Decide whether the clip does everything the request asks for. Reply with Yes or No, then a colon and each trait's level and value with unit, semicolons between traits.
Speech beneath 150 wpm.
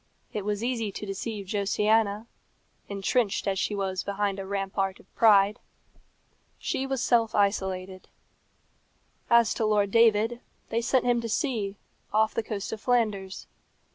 Yes: average, 140 wpm